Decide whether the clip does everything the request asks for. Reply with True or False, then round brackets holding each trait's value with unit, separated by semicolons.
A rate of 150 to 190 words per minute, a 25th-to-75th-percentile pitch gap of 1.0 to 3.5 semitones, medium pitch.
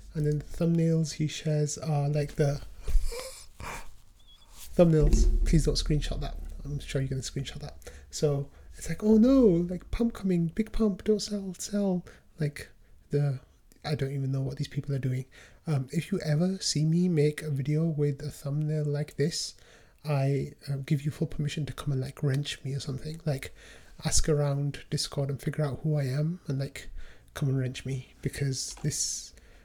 True (185 wpm; 2.7 semitones; 150 Hz)